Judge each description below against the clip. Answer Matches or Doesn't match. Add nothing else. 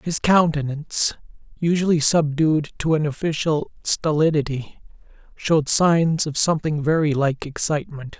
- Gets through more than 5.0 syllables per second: Doesn't match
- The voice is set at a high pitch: Doesn't match